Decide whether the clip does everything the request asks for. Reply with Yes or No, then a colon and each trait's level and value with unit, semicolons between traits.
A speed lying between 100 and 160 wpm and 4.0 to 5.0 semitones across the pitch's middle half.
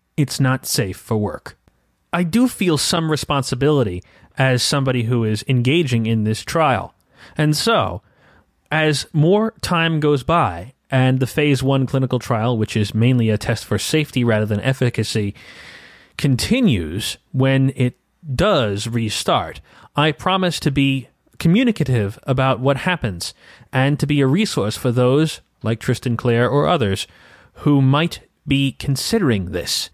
Yes: average, 140 wpm; average, 4.4 semitones